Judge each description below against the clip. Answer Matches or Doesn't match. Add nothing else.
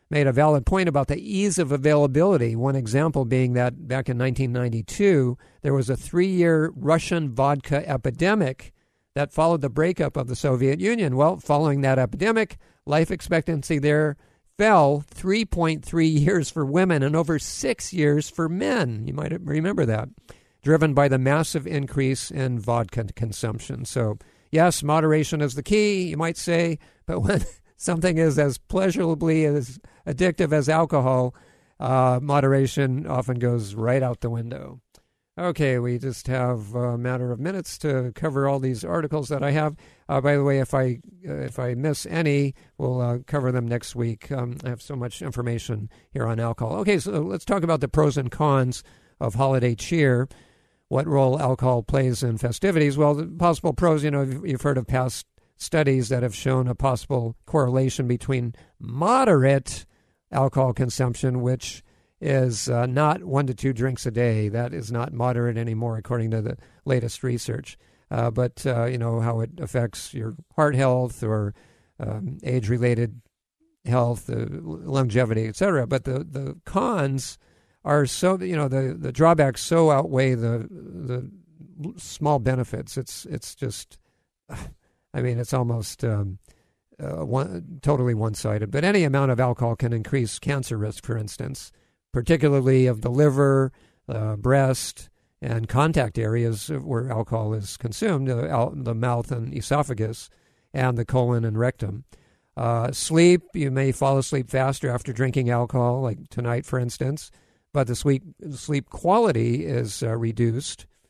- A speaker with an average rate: Matches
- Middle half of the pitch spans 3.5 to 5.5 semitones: Matches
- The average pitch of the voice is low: Matches